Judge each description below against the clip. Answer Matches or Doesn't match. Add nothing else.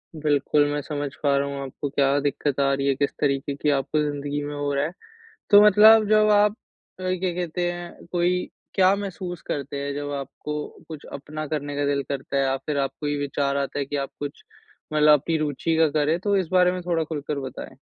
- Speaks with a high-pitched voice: Doesn't match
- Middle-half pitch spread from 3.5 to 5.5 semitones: Matches